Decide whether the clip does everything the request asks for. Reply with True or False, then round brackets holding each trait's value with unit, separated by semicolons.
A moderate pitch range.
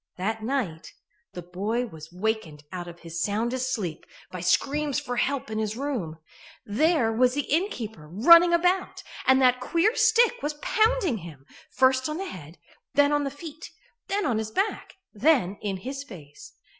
False (8.1 semitones)